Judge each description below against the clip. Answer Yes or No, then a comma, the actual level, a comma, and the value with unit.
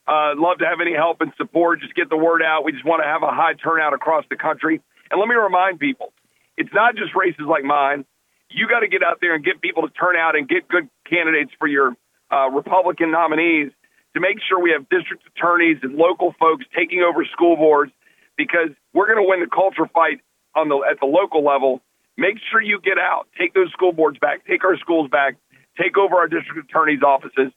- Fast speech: Yes, fast, 230 wpm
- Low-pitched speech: No, medium, 165 Hz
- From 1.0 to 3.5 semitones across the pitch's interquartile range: Yes, average, 2.8 semitones